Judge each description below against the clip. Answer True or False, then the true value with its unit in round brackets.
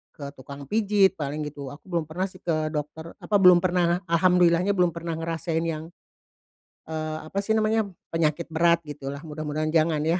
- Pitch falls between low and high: True (165 Hz)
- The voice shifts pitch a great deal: False (2.5 semitones)